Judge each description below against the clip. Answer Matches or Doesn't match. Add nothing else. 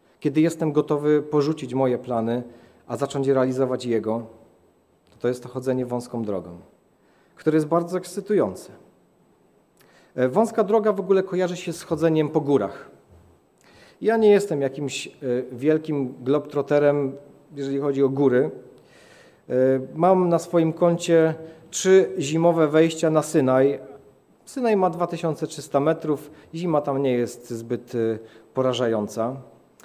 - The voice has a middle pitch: Matches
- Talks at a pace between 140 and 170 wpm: Doesn't match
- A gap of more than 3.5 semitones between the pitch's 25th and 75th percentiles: Matches